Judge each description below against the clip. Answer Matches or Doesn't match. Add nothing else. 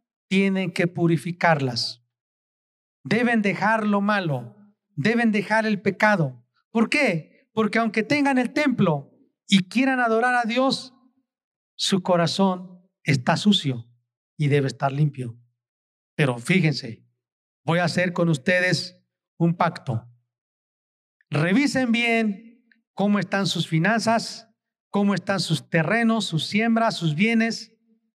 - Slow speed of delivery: Matches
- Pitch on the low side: Doesn't match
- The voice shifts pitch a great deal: Matches